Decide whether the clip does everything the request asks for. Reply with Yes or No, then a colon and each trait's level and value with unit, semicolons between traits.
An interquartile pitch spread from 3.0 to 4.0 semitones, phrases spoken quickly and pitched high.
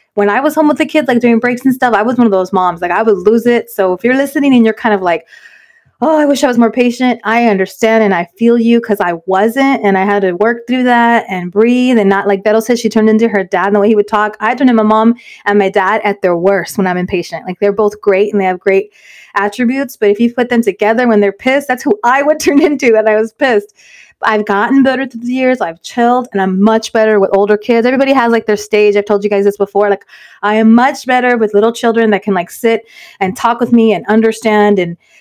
Yes: average, 3.3 semitones; fast, 275 wpm; high, 220 Hz